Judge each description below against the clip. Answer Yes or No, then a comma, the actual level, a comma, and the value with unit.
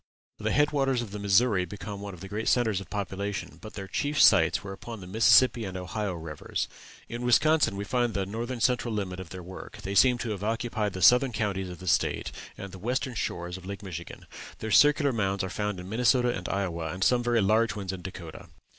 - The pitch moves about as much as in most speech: Yes, average, 4.2 semitones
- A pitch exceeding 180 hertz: No, low, 100 Hz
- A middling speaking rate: No, fast, 225 wpm